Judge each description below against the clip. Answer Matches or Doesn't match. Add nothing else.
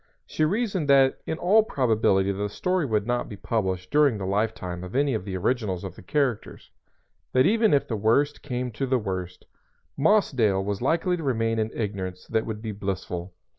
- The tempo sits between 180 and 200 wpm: Matches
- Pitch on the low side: Matches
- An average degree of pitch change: Doesn't match